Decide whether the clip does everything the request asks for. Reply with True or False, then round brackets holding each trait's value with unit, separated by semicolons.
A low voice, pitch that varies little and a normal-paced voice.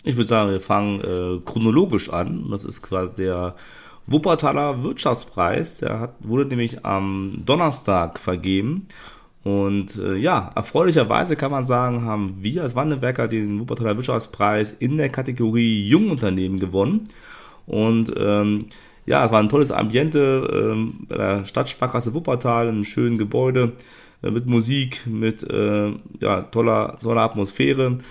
False (115 Hz; 3.9 semitones; 140 wpm)